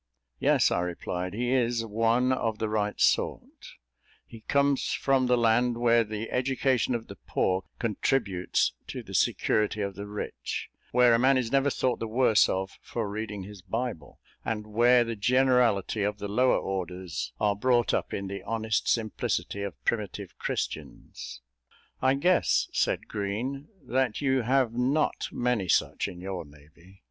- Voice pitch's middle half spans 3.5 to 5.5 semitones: Yes, average, 3.8 semitones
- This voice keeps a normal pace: Yes, average, 160 wpm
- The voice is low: Yes, low, 115 Hz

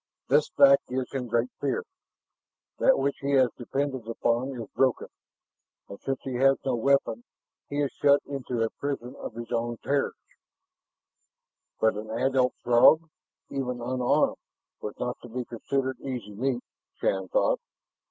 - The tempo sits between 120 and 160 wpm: Yes, average, 150 wpm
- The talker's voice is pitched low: Yes, low, 130 Hz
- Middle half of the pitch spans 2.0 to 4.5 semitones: Yes, narrow, 2.6 semitones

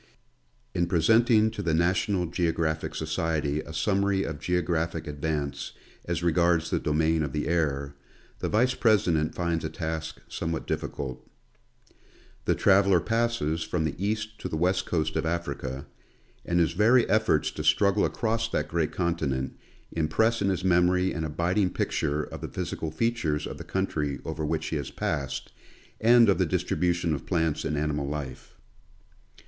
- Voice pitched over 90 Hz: No, very low, 85 Hz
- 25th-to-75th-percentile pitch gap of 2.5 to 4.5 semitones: Yes, average, 3.7 semitones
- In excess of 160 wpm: No, average, 155 wpm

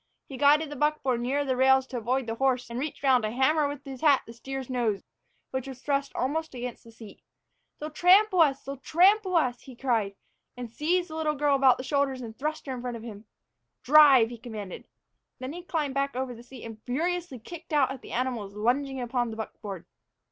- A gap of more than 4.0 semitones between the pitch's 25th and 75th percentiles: No, average, 3.5 semitones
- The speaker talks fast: Yes, fast, 220 wpm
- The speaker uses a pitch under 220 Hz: No, very high, 265 Hz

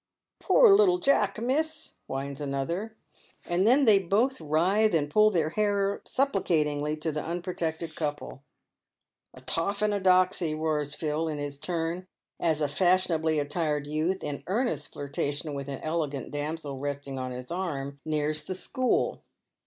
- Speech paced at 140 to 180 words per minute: Yes, average, 150 wpm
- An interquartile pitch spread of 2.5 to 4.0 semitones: No, average, 4.9 semitones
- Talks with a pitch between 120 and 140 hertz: No, medium, 160 Hz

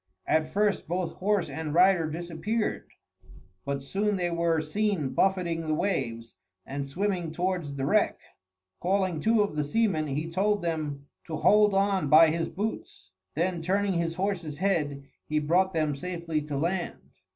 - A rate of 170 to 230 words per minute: No, average, 155 wpm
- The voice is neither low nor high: Yes, medium, 170 Hz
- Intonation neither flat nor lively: Yes, average, 4.0 semitones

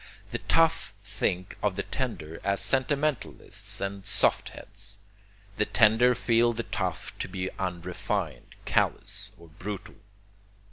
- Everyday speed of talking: No, slow, 125 wpm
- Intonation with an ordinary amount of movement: Yes, average, 4.2 semitones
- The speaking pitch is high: No, low, 100 Hz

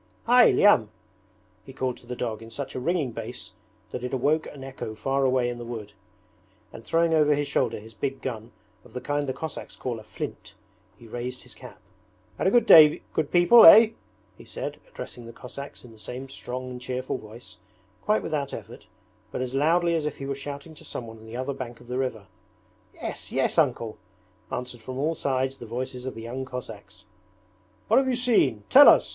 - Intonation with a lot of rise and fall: No, average, 3.5 semitones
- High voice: No, low, 130 Hz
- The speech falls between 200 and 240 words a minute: Yes, fast, 205 wpm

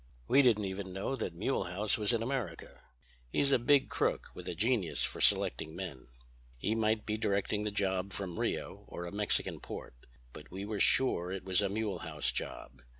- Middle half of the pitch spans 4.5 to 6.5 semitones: No, average, 3.3 semitones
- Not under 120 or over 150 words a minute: No, average, 185 wpm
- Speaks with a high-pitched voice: No, low, 100 Hz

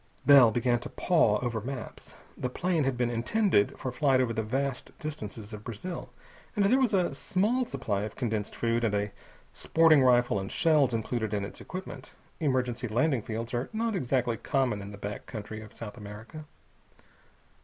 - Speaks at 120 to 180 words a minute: Yes, average, 175 wpm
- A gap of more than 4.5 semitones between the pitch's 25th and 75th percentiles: Yes, wide, 5.5 semitones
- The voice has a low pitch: Yes, low, 125 Hz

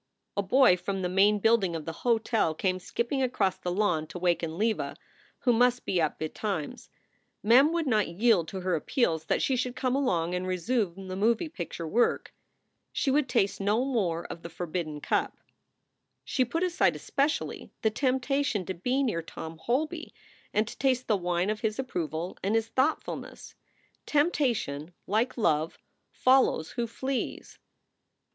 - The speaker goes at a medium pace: Yes, average, 165 wpm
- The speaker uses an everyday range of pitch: No, wide, 6.3 semitones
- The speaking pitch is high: Yes, high, 210 Hz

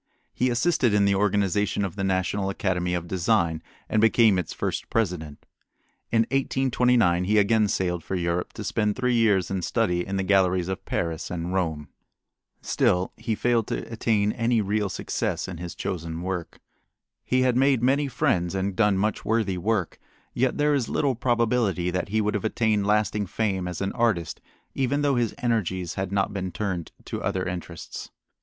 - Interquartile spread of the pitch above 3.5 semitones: Yes, average, 4.0 semitones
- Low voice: Yes, low, 100 Hz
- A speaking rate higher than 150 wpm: Yes, average, 175 wpm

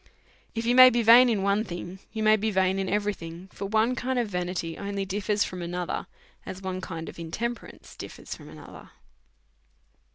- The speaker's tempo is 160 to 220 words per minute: Yes, average, 190 wpm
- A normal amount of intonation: Yes, average, 3.4 semitones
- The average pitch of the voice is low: No, high, 200 Hz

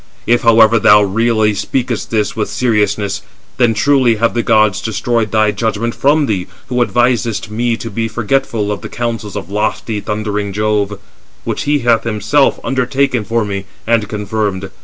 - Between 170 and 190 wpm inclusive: No, average, 160 wpm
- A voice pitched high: No, low, 110 Hz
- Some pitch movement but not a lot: No, narrow, 2.3 semitones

